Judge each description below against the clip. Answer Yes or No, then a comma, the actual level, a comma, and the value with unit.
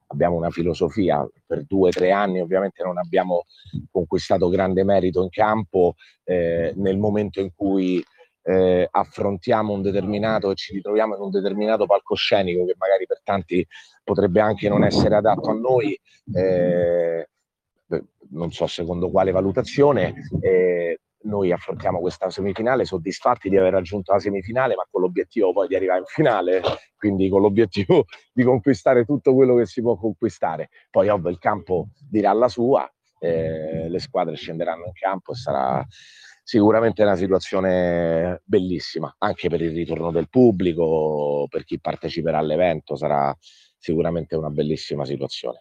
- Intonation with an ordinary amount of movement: Yes, average, 3.3 semitones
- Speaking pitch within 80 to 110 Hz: Yes, very low, 95 Hz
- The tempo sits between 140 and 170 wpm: Yes, average, 145 wpm